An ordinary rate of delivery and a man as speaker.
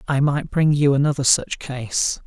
Yes: average, 185 wpm; male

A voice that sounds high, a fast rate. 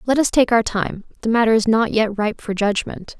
Yes: high, 220 Hz; fast, 245 wpm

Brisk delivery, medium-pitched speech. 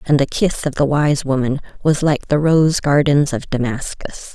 No: average, 195 wpm; medium, 145 Hz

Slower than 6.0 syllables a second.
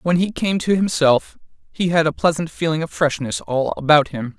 Yes: 5.0 syllables/s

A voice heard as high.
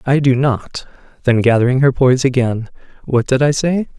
No: low, 130 Hz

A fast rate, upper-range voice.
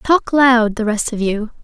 Yes: fast, 220 wpm; high, 235 Hz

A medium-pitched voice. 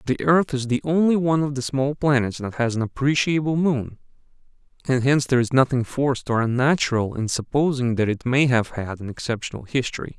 No: low, 130 Hz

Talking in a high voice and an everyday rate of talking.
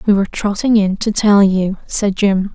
No: high, 200 Hz; fast, 210 wpm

